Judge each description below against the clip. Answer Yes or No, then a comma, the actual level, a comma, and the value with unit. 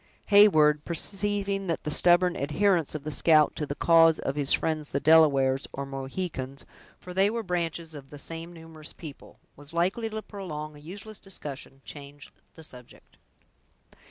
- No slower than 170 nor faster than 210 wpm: No, average, 160 wpm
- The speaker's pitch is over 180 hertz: No, medium, 160 Hz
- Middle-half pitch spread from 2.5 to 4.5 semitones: Yes, average, 3.9 semitones